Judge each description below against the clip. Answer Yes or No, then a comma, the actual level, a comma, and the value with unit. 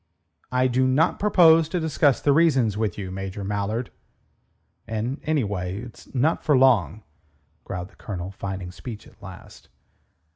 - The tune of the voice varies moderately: No, wide, 6.3 semitones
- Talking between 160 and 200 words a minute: No, average, 145 wpm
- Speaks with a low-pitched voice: Yes, low, 115 Hz